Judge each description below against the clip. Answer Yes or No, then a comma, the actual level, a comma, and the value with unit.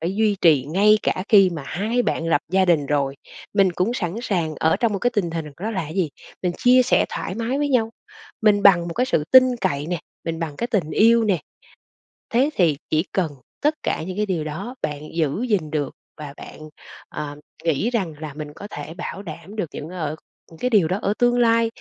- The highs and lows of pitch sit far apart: Yes, wide, 5.8 semitones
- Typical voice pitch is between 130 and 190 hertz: Yes, medium, 185 Hz